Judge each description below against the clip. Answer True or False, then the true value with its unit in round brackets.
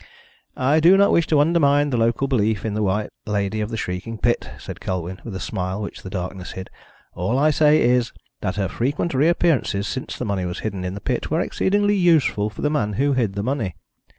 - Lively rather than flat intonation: True (6.5 semitones)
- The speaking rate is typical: False (220 wpm)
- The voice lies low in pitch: True (115 Hz)